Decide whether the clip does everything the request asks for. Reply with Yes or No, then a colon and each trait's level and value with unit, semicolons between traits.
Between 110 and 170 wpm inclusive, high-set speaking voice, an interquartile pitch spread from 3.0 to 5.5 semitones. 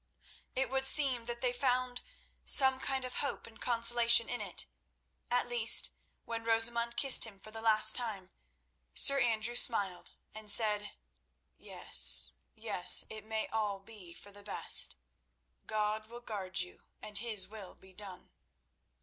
No: average, 145 wpm; high, 225 Hz; narrow, 2.6 semitones